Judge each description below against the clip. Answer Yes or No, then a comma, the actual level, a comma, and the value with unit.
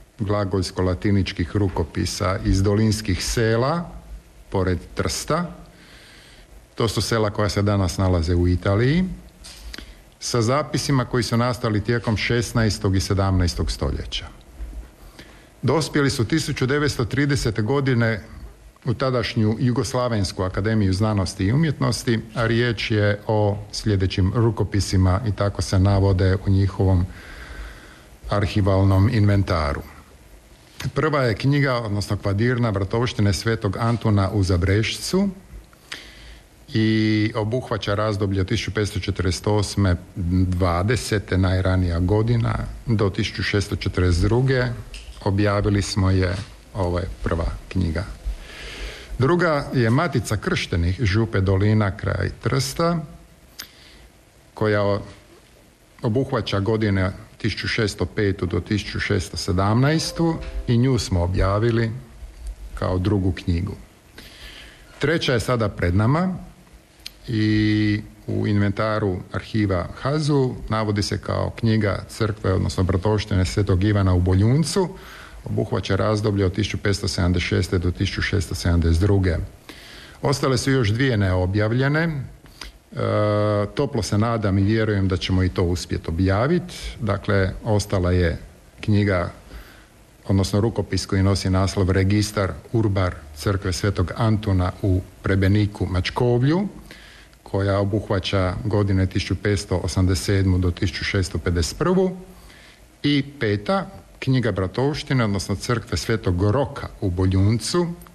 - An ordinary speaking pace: No, slow, 100 wpm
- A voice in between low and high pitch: No, low, 105 Hz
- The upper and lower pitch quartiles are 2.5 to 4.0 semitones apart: Yes, average, 3.5 semitones